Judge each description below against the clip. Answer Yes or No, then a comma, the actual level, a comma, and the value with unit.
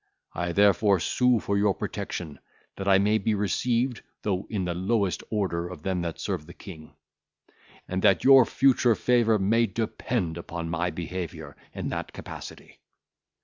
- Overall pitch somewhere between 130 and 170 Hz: No, very low, 95 Hz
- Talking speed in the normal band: Yes, average, 155 wpm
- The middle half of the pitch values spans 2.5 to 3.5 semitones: No, average, 4.2 semitones